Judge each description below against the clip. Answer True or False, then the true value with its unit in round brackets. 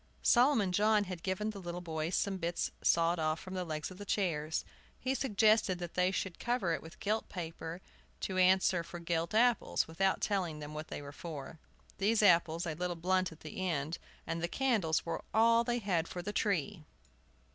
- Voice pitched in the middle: True (180 Hz)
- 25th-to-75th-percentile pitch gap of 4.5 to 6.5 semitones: False (3.7 semitones)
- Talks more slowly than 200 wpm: False (205 wpm)